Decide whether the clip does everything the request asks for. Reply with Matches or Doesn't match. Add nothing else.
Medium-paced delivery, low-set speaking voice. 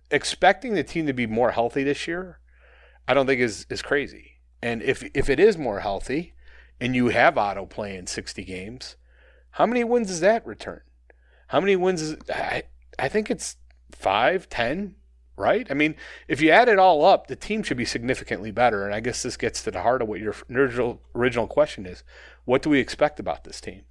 Doesn't match